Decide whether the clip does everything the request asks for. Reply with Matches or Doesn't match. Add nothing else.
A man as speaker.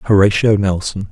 Matches